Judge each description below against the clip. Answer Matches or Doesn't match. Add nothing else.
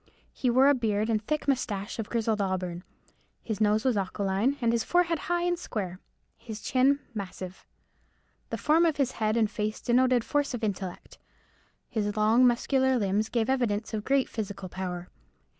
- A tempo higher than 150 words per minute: Matches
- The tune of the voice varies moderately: Matches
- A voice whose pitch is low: Doesn't match